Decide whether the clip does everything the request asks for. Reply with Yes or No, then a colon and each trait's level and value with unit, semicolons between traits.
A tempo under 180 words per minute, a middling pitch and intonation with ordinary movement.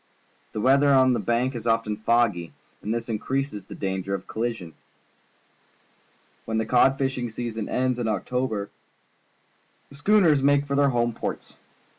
No: average, 155 wpm; low, 120 Hz; average, 3.4 semitones